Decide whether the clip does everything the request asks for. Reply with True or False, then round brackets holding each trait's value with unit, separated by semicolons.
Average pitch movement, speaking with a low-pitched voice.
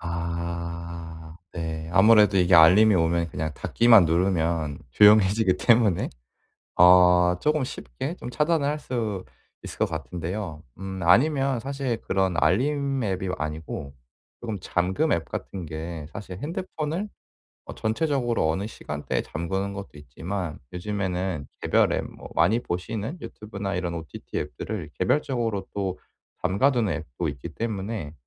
True (5.0 semitones; 95 Hz)